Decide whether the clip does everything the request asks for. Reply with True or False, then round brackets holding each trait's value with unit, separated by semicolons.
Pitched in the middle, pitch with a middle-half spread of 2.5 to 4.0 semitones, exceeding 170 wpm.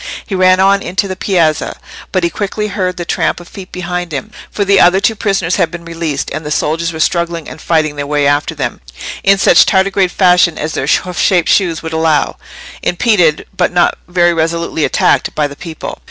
True (175 Hz; 2.8 semitones; 200 wpm)